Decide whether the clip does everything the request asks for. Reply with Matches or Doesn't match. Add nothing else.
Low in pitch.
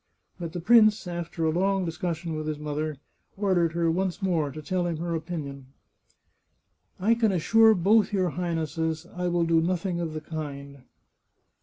Doesn't match